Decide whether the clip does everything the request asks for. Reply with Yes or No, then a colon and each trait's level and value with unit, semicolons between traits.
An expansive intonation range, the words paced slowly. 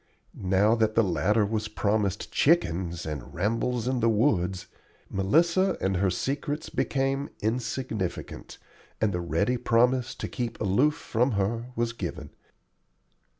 No: average, 4.7 semitones; slow, 130 wpm